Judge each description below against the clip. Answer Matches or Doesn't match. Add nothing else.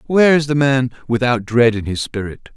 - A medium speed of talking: Doesn't match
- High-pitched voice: Doesn't match